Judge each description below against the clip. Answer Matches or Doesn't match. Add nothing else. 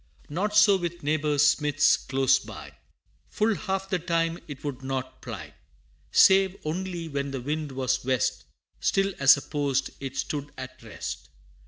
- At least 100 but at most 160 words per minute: Matches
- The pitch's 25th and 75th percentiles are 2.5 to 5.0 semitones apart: Matches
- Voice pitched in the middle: Matches